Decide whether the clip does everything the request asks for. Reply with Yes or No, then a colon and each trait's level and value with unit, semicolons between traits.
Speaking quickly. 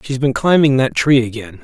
Yes: fast, 260 wpm